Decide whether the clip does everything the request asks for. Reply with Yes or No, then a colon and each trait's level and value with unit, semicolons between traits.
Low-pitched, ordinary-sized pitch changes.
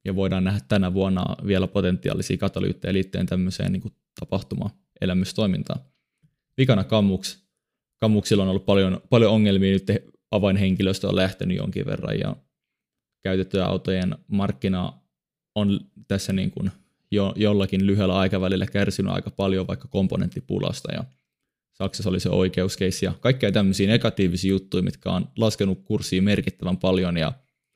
No: very low, 95 Hz; narrow, 1.5 semitones